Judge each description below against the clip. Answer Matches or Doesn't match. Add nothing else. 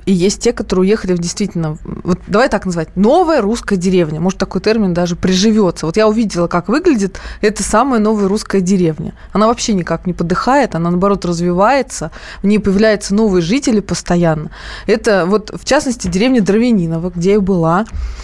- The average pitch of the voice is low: Doesn't match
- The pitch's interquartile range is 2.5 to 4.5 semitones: Matches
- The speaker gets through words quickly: Matches